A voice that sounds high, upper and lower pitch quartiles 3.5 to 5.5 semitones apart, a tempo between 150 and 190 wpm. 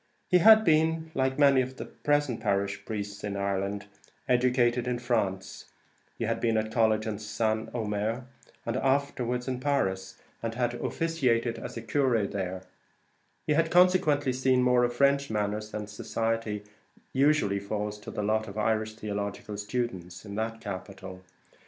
No: low, 115 Hz; average, 4.0 semitones; average, 160 wpm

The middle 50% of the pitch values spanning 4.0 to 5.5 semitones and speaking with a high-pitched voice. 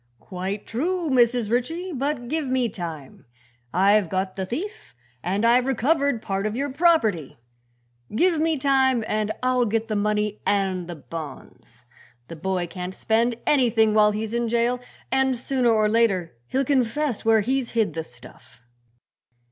Yes: average, 5.2 semitones; high, 225 Hz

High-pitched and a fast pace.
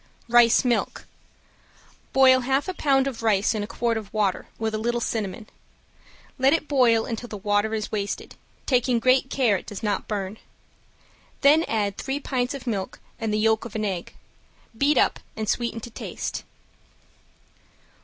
No: high, 230 Hz; average, 165 wpm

